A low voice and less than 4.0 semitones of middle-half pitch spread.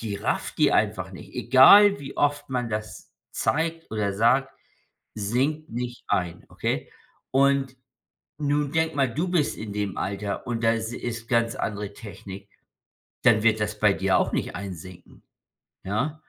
No: low, 115 Hz; average, 5.2 semitones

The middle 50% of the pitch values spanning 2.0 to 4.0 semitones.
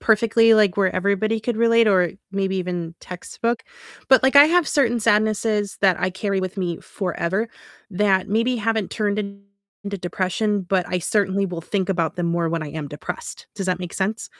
Yes: average, 3.1 semitones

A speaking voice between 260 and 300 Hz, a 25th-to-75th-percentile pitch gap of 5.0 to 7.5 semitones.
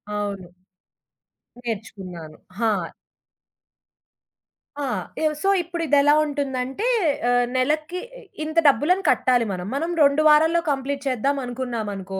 Yes: very high, 265 Hz; average, 5.3 semitones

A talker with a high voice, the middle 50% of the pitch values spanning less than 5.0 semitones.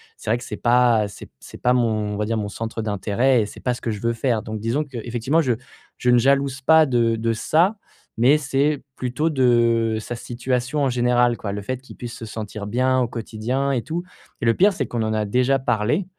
No: low, 120 Hz; average, 2.8 semitones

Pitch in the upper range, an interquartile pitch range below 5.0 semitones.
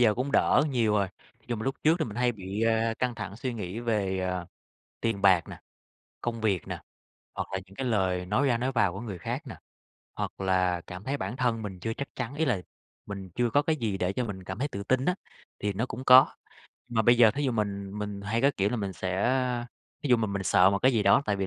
No: low, 110 Hz; average, 4.2 semitones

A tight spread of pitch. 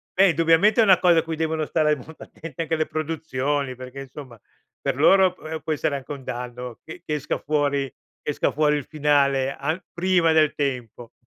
No: average, 3.0 semitones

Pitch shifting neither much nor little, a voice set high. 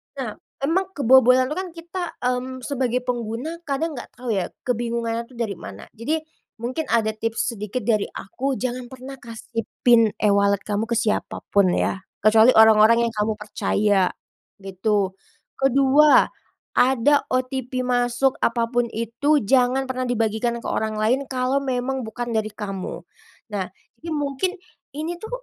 Yes: average, 3.3 semitones; high, 240 Hz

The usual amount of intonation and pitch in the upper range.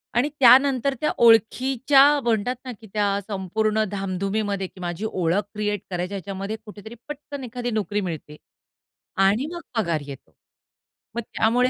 Yes: average, 4.0 semitones; high, 215 Hz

